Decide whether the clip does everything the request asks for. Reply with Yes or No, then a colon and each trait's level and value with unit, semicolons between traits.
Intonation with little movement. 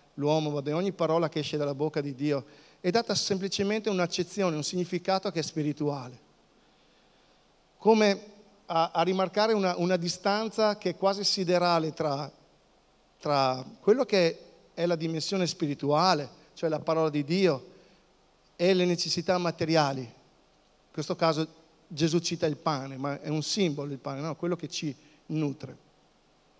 No: average, 3.6 semitones